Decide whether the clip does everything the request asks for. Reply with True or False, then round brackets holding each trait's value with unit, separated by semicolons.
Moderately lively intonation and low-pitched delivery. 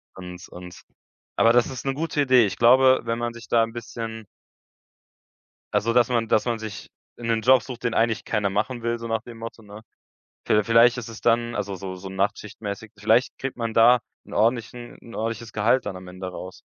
False (2.2 semitones; 115 Hz)